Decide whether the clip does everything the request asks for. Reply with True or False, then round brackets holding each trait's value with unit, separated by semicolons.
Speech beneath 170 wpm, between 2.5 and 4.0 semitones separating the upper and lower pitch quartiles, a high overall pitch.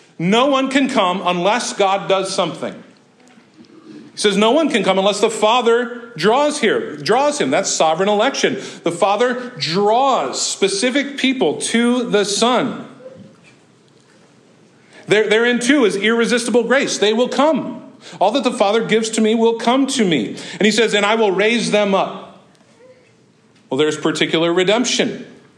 True (155 wpm; 3.4 semitones; 225 Hz)